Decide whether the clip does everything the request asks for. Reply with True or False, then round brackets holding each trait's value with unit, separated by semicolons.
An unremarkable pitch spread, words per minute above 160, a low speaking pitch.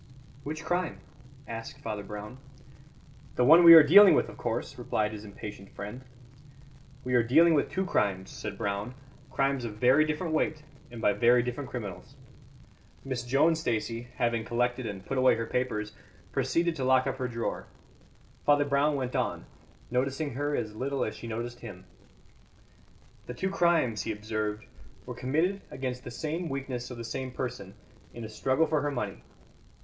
True (4.3 semitones; 170 wpm; 125 Hz)